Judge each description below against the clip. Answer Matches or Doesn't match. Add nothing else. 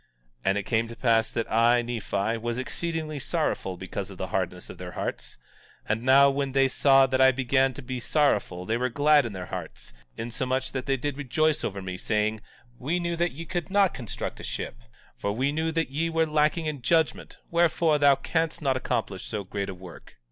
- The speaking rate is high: Matches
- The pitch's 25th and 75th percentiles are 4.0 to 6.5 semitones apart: Matches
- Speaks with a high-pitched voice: Doesn't match